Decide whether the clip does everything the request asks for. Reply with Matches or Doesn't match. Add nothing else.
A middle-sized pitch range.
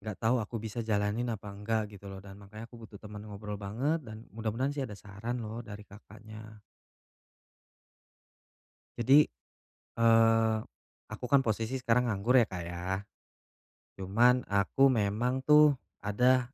Matches